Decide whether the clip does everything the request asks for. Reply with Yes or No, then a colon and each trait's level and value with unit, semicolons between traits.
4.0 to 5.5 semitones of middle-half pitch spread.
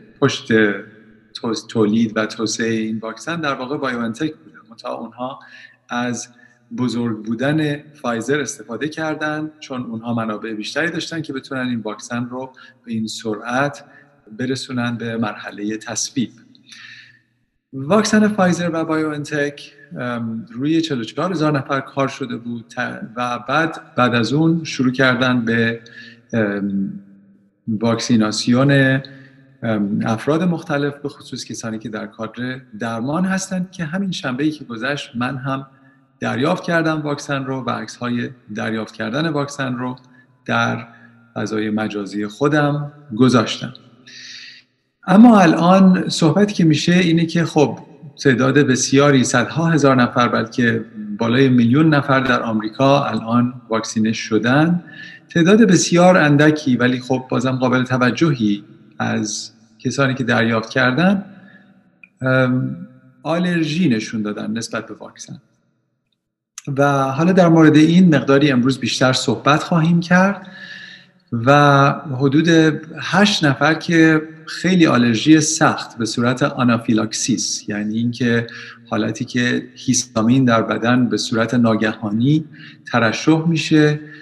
Yes: average, 4.8 semitones